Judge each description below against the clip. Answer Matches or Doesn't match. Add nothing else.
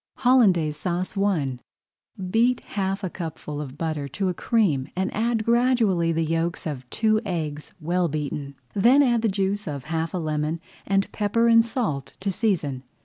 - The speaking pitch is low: Doesn't match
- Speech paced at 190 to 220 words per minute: Doesn't match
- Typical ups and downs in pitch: Doesn't match